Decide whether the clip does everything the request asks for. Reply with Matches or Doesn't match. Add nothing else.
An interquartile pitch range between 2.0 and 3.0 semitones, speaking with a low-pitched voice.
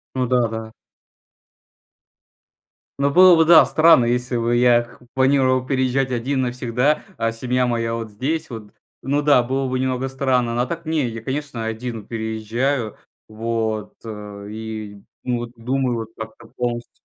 Matches